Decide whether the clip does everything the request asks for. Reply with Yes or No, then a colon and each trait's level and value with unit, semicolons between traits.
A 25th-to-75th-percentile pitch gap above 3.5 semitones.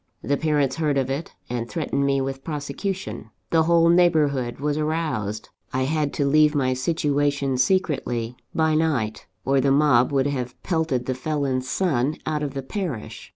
No: average, 3.2 semitones